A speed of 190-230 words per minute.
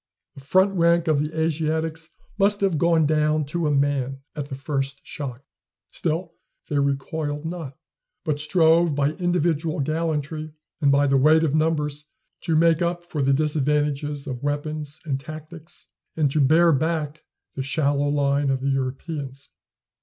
No: average, 155 wpm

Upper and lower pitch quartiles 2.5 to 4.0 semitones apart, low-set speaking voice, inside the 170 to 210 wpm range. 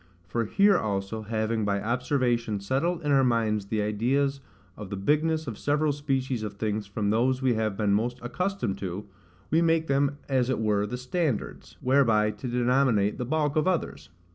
No: average, 4.8 semitones; low, 120 Hz; average, 180 wpm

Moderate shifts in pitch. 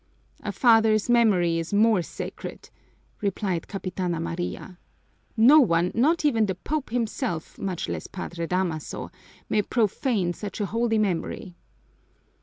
Yes: average, 4.5 semitones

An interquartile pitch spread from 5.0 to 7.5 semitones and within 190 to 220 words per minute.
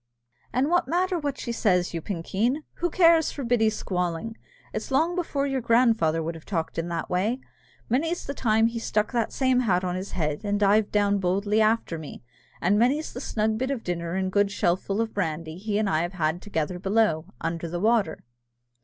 Yes: wide, 5.6 semitones; average, 200 wpm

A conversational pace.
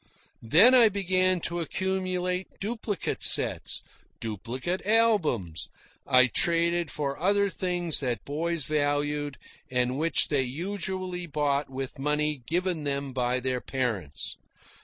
No: slow, 115 wpm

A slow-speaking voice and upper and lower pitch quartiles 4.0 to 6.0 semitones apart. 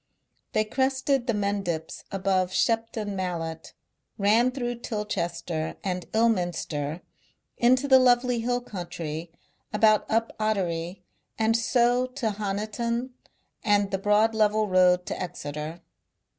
Yes: slow, 115 wpm; average, 4.6 semitones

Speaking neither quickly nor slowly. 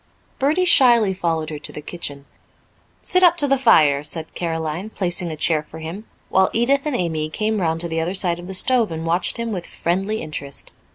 No: fast, 210 wpm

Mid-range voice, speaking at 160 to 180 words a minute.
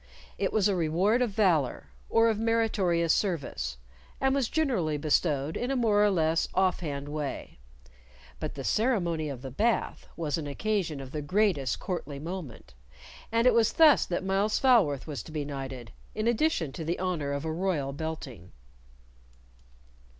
Yes: medium, 170 Hz; average, 165 wpm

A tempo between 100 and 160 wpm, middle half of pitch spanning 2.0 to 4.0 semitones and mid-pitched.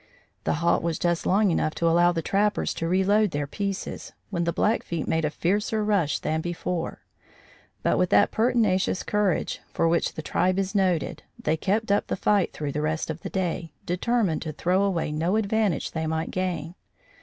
No: average, 190 wpm; average, 3.6 semitones; medium, 175 Hz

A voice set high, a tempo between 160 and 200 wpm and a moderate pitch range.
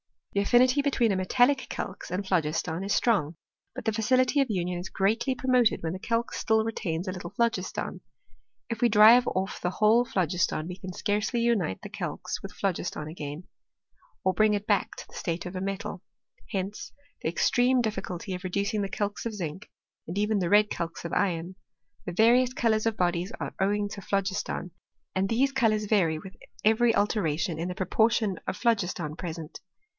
Yes: high, 200 Hz; average, 185 wpm; average, 4.0 semitones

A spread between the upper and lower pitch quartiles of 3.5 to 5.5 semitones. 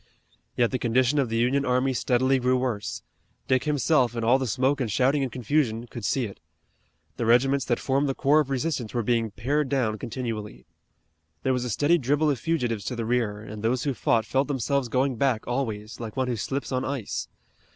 No: average, 2.9 semitones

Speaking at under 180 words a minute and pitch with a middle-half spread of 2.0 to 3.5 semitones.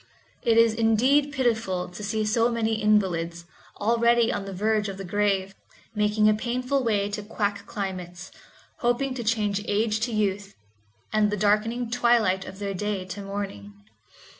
Yes: average, 160 wpm; narrow, 2.6 semitones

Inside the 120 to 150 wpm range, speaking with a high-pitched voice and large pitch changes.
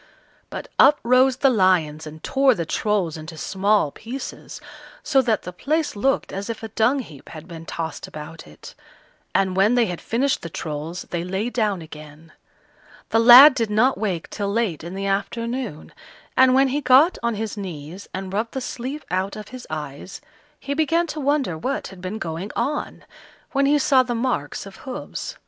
No: average, 185 wpm; high, 210 Hz; wide, 6.9 semitones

